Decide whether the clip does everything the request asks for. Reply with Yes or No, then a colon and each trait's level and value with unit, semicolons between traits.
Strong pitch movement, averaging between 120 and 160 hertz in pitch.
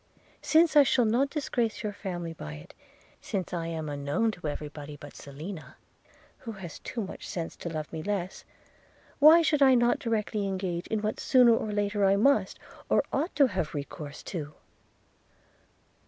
No: wide, 6.6 semitones; high, 195 Hz